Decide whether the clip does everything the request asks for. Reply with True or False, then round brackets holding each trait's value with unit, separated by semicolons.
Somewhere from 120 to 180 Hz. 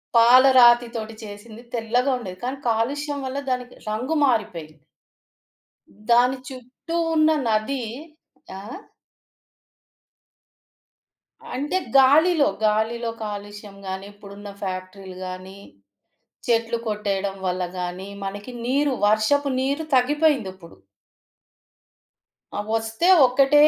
False (230 Hz)